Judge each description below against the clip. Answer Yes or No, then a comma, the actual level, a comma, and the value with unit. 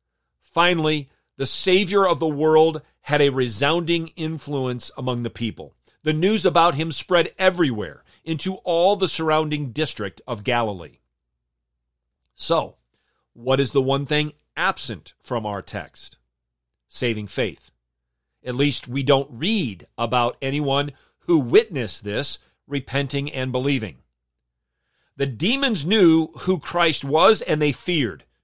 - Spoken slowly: Yes, slow, 125 wpm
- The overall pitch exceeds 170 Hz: No, medium, 140 Hz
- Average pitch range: No, wide, 6.5 semitones